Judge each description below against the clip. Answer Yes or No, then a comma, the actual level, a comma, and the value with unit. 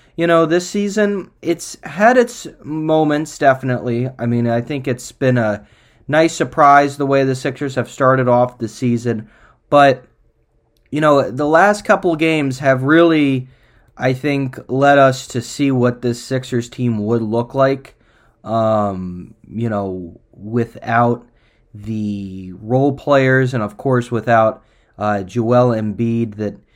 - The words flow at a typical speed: Yes, average, 145 wpm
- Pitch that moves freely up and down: No, average, 3.8 semitones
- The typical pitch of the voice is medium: No, low, 125 Hz